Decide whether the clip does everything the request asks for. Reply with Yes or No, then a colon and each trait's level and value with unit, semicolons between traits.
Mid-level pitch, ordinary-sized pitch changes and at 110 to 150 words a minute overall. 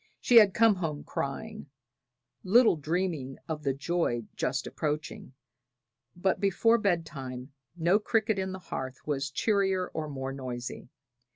No: medium, 165 Hz; wide, 6.2 semitones; slow, 135 wpm